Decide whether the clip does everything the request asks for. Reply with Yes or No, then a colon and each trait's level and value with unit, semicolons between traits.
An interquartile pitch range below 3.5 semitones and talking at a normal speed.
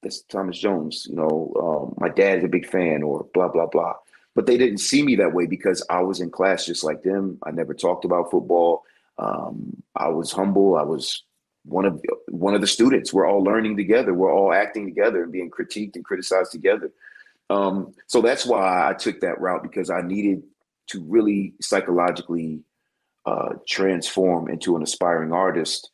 Yes: average, 2.9 semitones; average, 190 wpm